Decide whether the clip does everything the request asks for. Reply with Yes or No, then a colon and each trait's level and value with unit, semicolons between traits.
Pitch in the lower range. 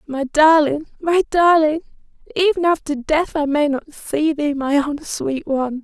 No: very high, 300 Hz